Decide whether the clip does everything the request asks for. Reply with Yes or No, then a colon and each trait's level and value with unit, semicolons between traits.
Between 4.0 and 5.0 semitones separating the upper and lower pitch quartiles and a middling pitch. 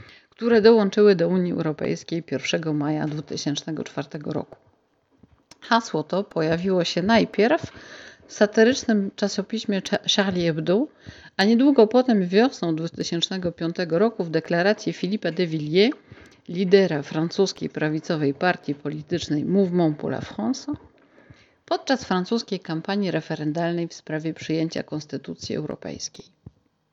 Yes: average, 4.7 semitones; medium, 180 Hz